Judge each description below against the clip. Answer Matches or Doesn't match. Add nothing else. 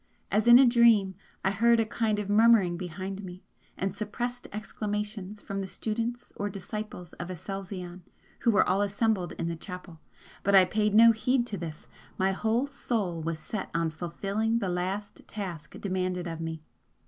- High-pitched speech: Matches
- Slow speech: Doesn't match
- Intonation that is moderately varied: Matches